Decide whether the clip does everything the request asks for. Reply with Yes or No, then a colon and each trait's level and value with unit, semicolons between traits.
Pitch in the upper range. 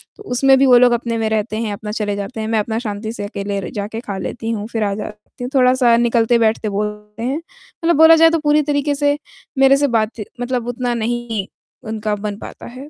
Yes: high, 230 Hz